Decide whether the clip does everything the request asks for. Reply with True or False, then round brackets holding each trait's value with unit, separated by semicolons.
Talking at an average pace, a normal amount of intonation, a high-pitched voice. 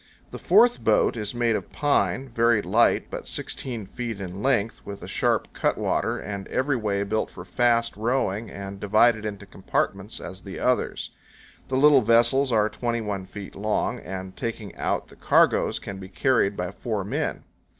False (170 wpm; 3.4 semitones; 110 Hz)